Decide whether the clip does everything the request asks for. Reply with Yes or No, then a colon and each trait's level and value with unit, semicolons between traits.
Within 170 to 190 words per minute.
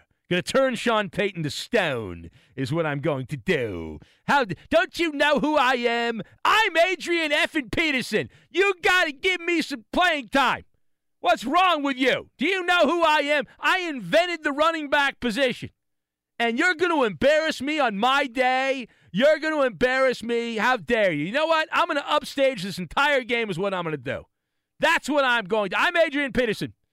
Yes: average, 185 wpm